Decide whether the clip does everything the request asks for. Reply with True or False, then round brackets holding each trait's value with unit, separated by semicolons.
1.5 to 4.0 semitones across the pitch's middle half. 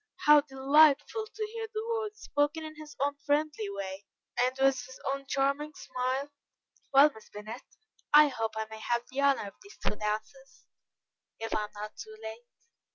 False (5.1 semitones)